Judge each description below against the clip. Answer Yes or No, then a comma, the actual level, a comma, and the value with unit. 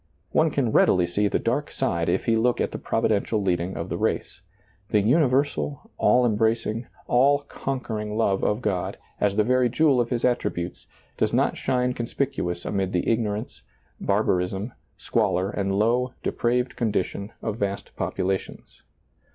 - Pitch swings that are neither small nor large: Yes, average, 4.0 semitones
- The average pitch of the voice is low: Yes, low, 110 Hz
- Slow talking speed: No, average, 155 wpm